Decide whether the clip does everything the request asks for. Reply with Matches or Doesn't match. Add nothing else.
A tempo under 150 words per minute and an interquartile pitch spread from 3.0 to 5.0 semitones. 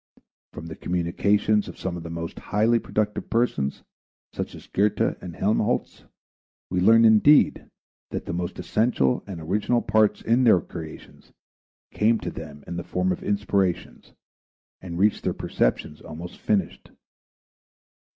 Matches